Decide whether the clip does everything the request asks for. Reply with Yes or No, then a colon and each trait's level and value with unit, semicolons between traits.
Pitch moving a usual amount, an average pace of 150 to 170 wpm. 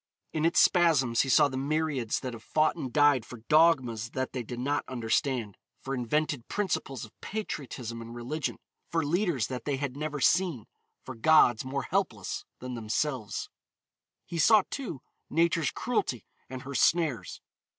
Yes: average, 4.5 semitones; average, 160 wpm